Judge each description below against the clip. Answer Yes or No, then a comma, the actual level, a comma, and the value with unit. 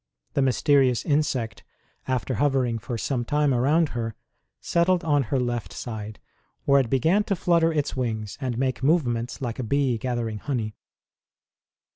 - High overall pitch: No, low, 130 Hz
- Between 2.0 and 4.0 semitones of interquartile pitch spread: Yes, average, 3.7 semitones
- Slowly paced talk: No, average, 150 wpm